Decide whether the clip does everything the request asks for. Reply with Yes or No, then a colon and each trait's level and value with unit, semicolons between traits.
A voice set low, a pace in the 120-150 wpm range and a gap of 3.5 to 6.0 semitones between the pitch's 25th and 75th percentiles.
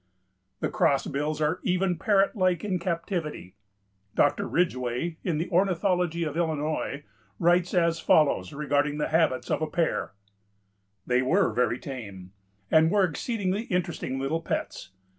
No: medium, 160 Hz; slow, 135 wpm; average, 3.8 semitones